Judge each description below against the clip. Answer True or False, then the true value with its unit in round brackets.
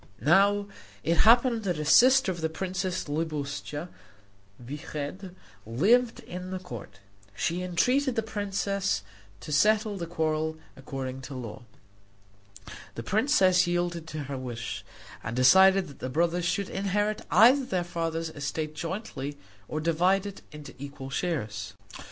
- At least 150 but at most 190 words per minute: False (135 wpm)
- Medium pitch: True (170 Hz)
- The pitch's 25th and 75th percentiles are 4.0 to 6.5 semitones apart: True (5.1 semitones)